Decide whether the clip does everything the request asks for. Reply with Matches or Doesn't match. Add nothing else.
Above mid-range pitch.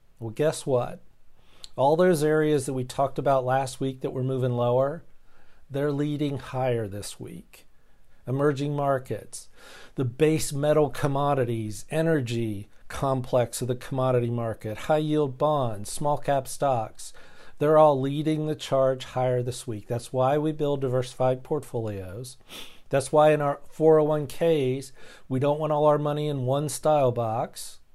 Doesn't match